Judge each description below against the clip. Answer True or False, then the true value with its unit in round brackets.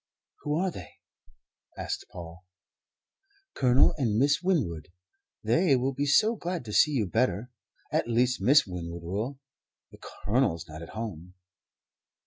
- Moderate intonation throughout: False (7.7 semitones)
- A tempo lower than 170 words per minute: True (135 wpm)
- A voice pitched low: True (120 Hz)